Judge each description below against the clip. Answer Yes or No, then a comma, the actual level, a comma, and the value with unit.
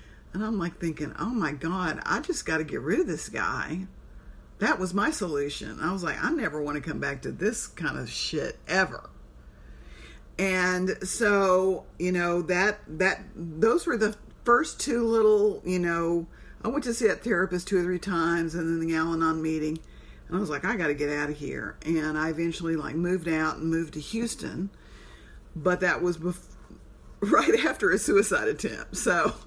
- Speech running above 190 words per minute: Yes, average, 200 wpm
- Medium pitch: Yes, medium, 170 Hz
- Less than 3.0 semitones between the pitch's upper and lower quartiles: No, average, 3.6 semitones